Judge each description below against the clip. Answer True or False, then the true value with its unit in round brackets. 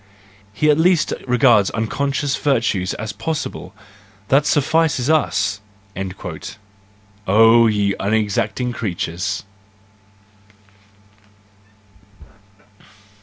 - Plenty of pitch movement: True (5.7 semitones)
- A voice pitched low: True (115 Hz)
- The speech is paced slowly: True (65 wpm)